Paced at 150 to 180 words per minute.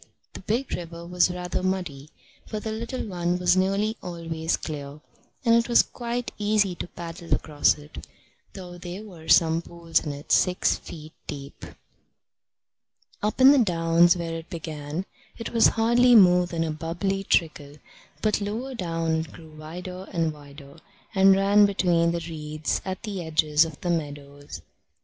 Yes: average, 160 wpm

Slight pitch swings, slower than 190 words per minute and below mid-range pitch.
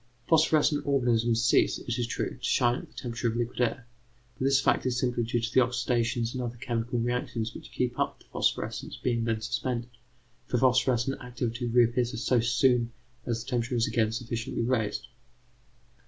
Yes: narrow, 1.3 semitones; average, 180 wpm; low, 120 Hz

